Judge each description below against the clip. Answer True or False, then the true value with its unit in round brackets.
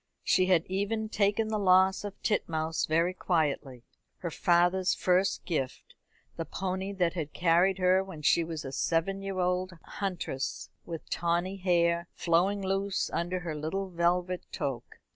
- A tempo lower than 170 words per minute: True (150 wpm)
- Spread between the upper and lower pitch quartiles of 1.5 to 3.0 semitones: True (2.4 semitones)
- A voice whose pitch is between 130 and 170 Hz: False (180 Hz)